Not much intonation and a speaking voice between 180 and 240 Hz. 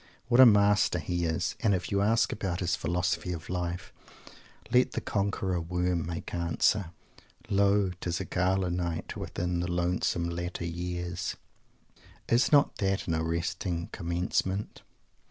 No: narrow, 2.3 semitones; very low, 90 Hz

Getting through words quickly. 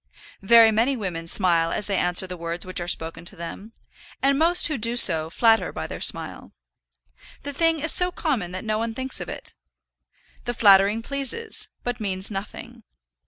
No: average, 180 wpm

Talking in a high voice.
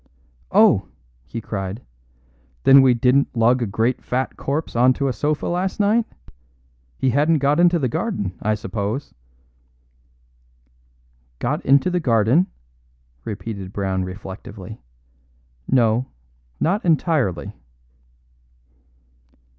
No: low, 125 Hz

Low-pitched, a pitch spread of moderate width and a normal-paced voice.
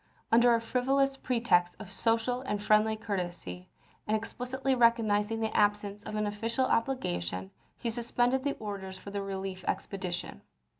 No: high, 215 Hz; average, 3.5 semitones; average, 145 wpm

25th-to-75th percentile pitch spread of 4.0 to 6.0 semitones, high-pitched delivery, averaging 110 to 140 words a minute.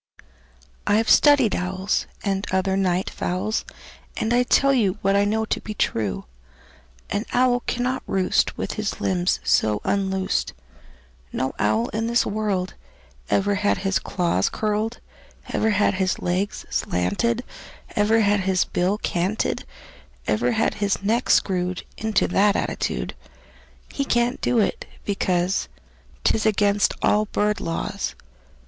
No: average, 2.9 semitones; high, 200 Hz; slow, 135 wpm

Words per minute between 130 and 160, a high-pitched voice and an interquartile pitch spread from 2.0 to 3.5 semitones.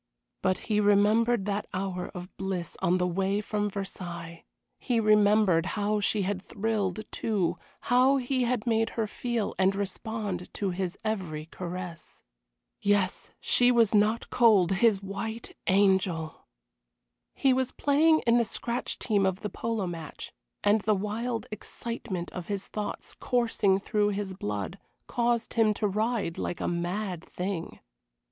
Yes: average, 145 wpm; high, 205 Hz; average, 3.2 semitones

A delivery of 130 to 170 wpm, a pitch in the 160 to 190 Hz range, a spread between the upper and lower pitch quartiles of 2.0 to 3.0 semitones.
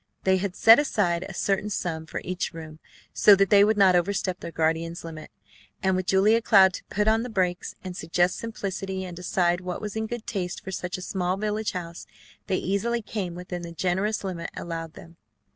No: fast, 205 wpm; medium, 185 Hz; average, 2.7 semitones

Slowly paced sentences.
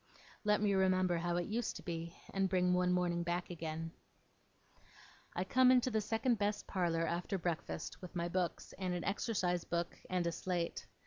No: average, 180 wpm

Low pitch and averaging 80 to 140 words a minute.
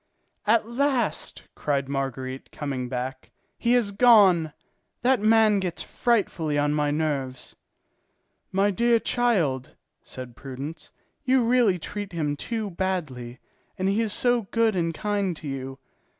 No: medium, 185 Hz; slow, 135 wpm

